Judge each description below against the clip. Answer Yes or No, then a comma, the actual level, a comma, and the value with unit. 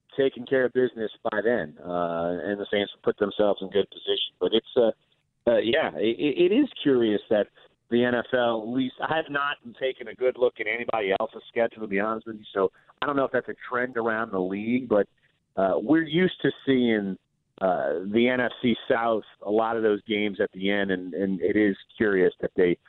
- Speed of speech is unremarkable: No, fast, 215 wpm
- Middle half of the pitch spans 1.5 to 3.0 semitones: No, average, 4.1 semitones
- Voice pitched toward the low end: Yes, low, 115 Hz